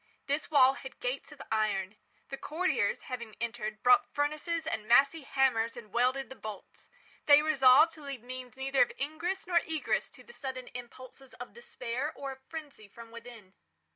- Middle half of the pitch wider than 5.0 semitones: No, average, 4.3 semitones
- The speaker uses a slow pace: No, average, 170 wpm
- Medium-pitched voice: No, very high, 265 Hz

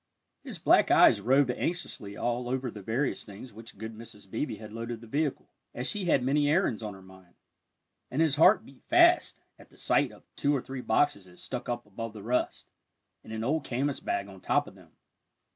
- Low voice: Yes, low, 120 Hz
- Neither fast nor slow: No, fast, 210 wpm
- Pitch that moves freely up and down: No, average, 4.7 semitones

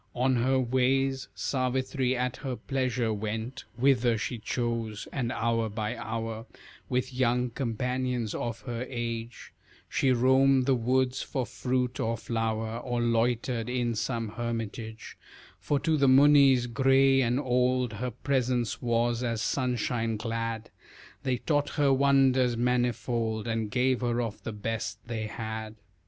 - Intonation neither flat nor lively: No, narrow, 2.3 semitones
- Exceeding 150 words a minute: No, average, 140 wpm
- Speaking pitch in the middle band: No, low, 120 Hz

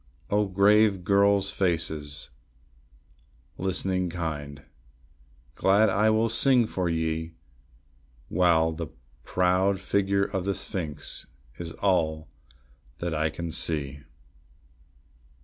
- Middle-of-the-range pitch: No, very low, 90 Hz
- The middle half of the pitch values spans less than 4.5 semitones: Yes, average, 3.6 semitones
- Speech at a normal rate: No, slow, 95 wpm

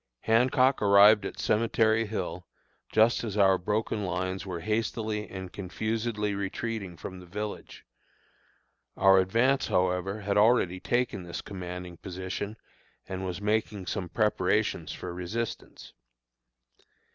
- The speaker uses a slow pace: Yes, slow, 120 wpm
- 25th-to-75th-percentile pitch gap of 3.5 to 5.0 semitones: No, average, 3.0 semitones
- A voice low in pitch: Yes, low, 100 Hz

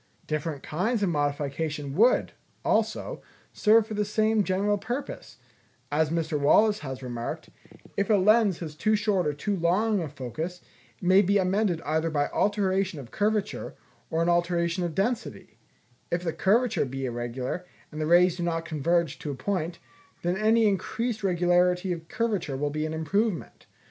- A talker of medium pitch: Yes, medium, 175 Hz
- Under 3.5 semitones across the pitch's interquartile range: No, average, 5.0 semitones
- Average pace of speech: Yes, average, 170 wpm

